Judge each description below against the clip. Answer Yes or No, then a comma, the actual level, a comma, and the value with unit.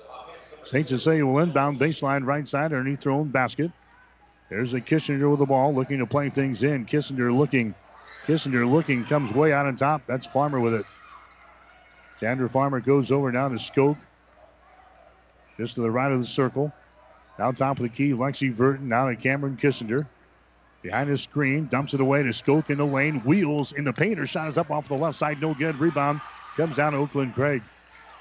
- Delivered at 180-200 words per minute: Yes, average, 190 wpm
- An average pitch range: No, narrow, 2.1 semitones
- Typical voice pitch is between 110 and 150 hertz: Yes, medium, 140 Hz